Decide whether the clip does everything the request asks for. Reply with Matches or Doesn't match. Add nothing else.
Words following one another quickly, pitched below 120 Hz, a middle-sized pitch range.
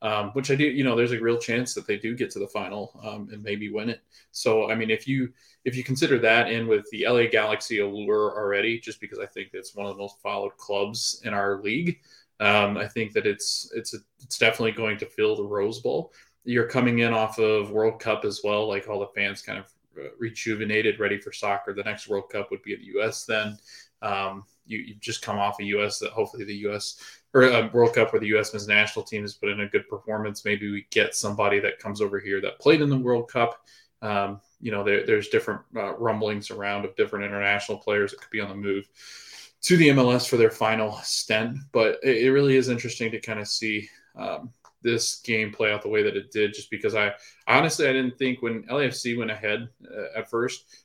Matches